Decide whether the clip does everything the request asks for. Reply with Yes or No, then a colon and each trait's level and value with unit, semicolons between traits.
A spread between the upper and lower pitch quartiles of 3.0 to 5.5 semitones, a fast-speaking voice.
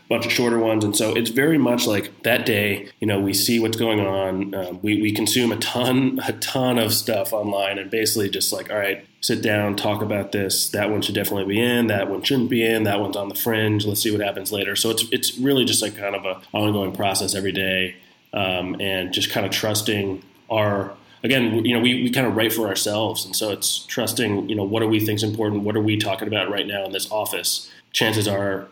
No: narrow, 2.4 semitones; fast, 240 wpm